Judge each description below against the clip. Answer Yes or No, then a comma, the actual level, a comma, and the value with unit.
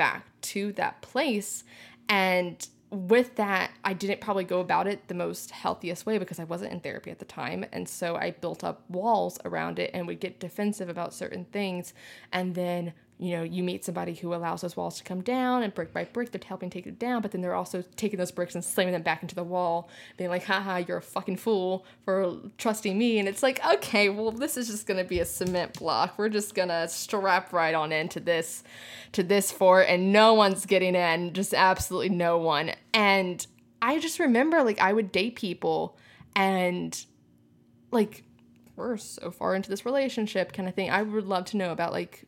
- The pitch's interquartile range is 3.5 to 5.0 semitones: No, average, 2.9 semitones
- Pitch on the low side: No, high, 190 Hz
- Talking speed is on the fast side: Yes, fast, 210 wpm